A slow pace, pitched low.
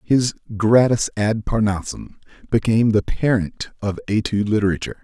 Yes: slow, 120 wpm; low, 105 Hz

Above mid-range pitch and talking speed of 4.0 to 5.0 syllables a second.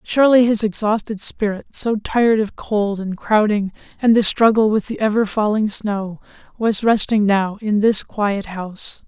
Yes: high, 210 Hz; 4.5 syllables/s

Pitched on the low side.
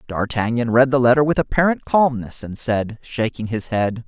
Yes: low, 120 Hz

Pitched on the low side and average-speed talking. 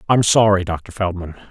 Yes: very low, 95 Hz; average, 160 wpm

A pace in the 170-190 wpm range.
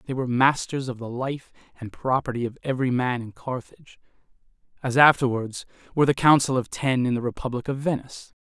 Yes: average, 180 wpm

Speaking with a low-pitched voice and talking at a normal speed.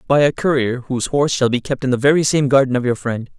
No: low, 130 Hz; fast, 285 wpm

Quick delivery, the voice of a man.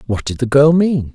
Yes: fast, 260 wpm; male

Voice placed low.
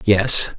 Yes: low, 105 Hz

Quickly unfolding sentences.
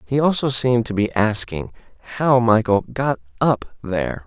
No: average, 155 wpm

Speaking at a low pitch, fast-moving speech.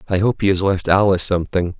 Yes: very low, 95 Hz; fast, 235 wpm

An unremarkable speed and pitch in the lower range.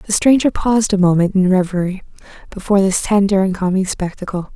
No: average, 170 wpm; high, 195 Hz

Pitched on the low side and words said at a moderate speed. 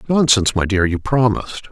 Yes: low, 110 Hz; average, 175 wpm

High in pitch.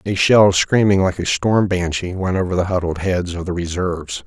No: very low, 90 Hz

